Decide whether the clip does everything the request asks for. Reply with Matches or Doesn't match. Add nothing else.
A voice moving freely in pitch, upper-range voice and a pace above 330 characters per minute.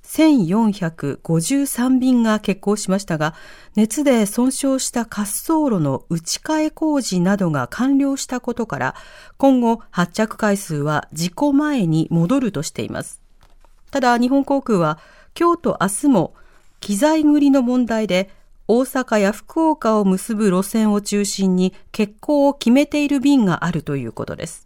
Doesn't match